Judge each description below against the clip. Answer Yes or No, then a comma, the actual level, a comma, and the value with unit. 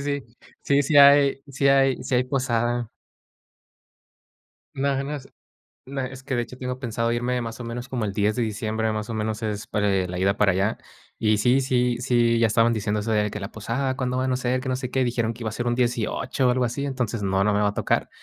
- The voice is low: Yes, low, 120 Hz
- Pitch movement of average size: Yes, average, 3.0 semitones